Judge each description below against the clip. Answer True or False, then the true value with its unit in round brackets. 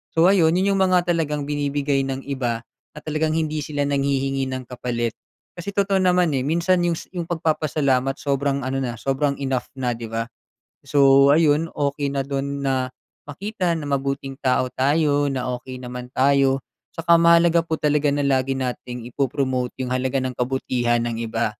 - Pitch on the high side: False (140 Hz)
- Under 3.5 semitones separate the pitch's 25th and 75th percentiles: True (3.1 semitones)